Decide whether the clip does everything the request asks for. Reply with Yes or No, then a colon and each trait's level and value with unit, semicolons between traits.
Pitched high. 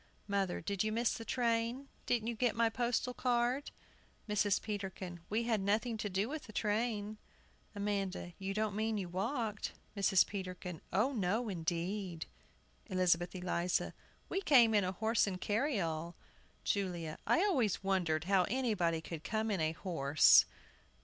Yes: high, 205 Hz